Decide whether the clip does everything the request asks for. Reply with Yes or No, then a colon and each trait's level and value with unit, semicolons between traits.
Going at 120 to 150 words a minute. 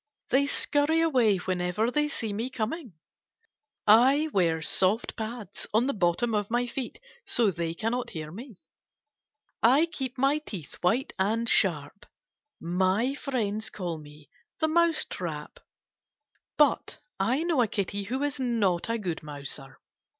Yes: average, 145 wpm